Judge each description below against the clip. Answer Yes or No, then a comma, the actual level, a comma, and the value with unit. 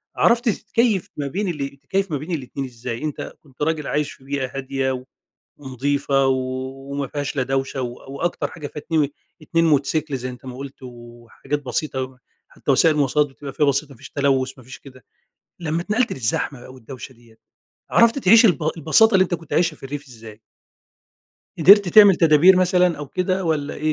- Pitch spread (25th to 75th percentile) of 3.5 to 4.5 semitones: Yes, average, 4.0 semitones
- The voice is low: No, medium, 145 Hz